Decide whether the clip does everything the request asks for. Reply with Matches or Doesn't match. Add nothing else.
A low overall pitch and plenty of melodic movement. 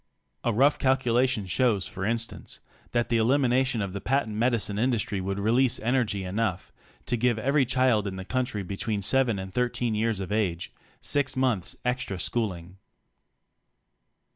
Doesn't match